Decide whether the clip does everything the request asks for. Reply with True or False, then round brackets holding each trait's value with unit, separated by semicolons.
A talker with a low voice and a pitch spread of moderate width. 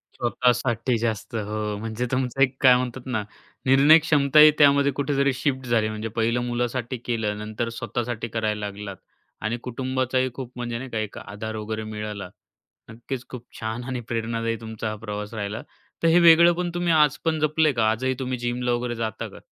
True (120 Hz; 3.1 semitones)